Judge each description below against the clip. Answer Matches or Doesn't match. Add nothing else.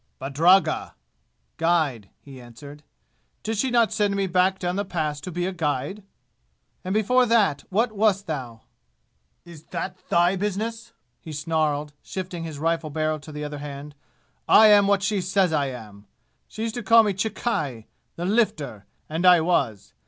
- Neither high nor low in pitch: Matches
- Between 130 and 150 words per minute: Doesn't match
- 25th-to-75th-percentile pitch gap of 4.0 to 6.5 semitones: Matches